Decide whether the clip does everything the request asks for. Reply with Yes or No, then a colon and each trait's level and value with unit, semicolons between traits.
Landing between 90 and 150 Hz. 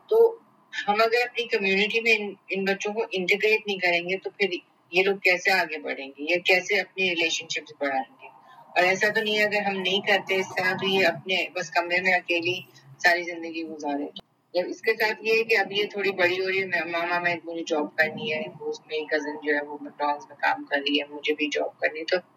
No: medium, 180 Hz